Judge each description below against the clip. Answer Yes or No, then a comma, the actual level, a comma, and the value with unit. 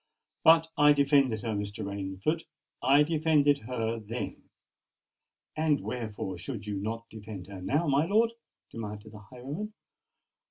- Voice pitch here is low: Yes, low, 120 Hz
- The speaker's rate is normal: No, slow, 125 wpm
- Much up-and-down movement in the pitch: Yes, wide, 6.0 semitones